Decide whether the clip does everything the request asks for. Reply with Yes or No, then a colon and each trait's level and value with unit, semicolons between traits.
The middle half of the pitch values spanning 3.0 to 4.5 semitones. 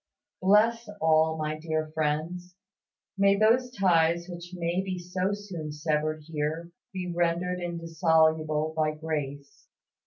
No: narrow, 2.5 semitones